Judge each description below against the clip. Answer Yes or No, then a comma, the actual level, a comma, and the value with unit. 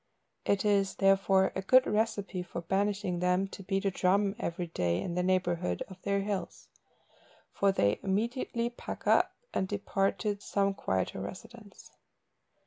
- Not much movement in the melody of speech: Yes, narrow, 2.0 semitones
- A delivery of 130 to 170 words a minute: Yes, average, 150 wpm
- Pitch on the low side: No, high, 195 Hz